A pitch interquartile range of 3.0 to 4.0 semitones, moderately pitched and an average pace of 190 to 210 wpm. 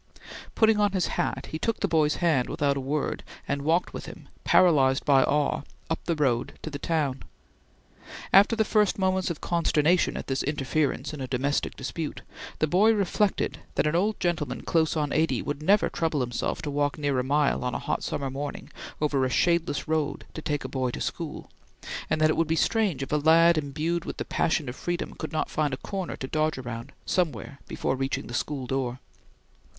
Yes: average, 3.6 semitones; medium, 150 Hz; fast, 205 wpm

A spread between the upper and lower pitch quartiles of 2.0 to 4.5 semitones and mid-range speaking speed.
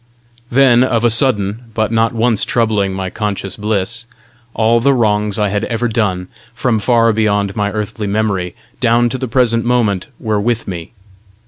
Yes: narrow, 2.4 semitones; average, 165 wpm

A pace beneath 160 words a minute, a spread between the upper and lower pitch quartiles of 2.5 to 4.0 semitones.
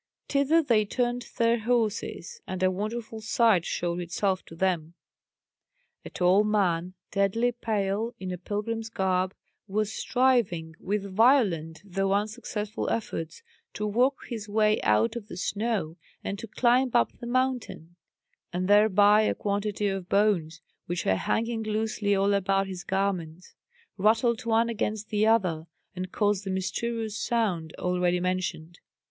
Yes: average, 140 wpm; average, 3.5 semitones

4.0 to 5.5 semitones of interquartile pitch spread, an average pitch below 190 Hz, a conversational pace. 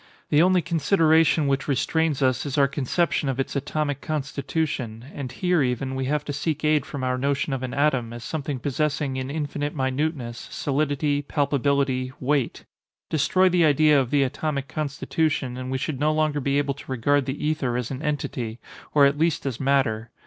No: narrow, 2.5 semitones; medium, 140 Hz; average, 185 wpm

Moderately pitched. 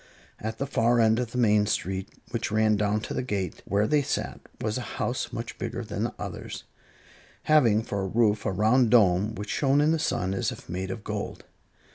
No: low, 110 Hz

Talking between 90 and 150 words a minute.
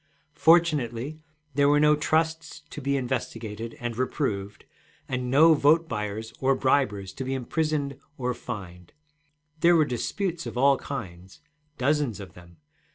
Yes: average, 140 wpm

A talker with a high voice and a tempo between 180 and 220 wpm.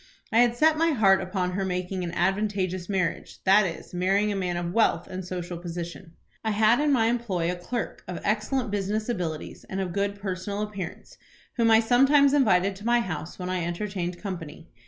Yes: high, 195 Hz; average, 195 wpm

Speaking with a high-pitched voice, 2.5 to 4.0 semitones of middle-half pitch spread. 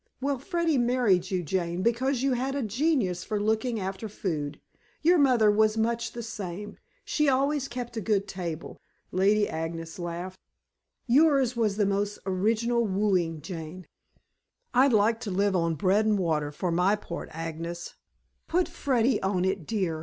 No: high, 210 Hz; average, 5.1 semitones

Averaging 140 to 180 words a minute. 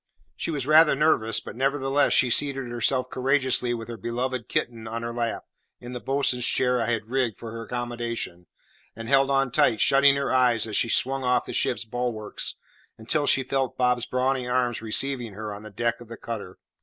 No: average, 195 wpm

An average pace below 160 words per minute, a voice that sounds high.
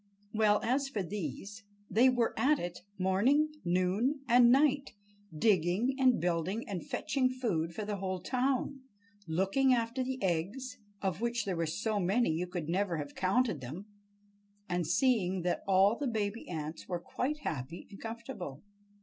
Yes: average, 150 wpm; high, 205 Hz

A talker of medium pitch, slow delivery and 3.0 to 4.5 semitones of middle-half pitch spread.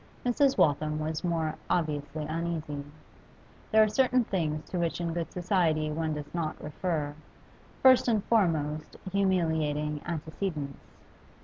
Yes: medium, 160 Hz; slow, 125 wpm; average, 3.3 semitones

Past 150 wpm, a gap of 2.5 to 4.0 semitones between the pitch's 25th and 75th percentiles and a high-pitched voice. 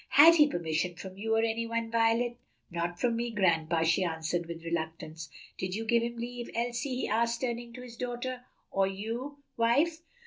No: average, 185 wpm; wide, 5.5 semitones; high, 230 Hz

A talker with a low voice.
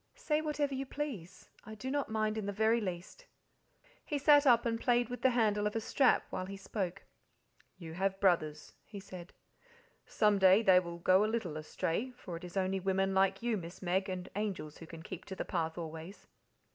No: high, 195 Hz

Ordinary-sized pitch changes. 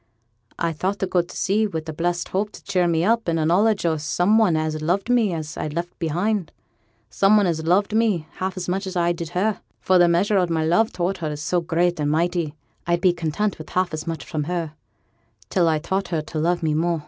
Yes: average, 3.0 semitones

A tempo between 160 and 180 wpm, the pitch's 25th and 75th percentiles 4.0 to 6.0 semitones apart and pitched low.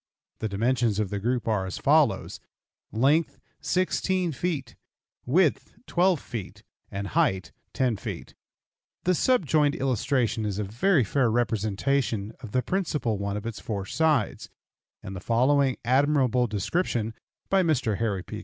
No: average, 140 wpm; wide, 5.5 semitones; low, 120 Hz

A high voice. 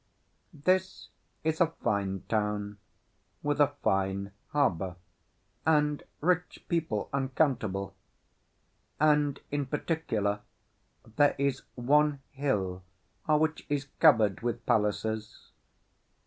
No: low, 135 Hz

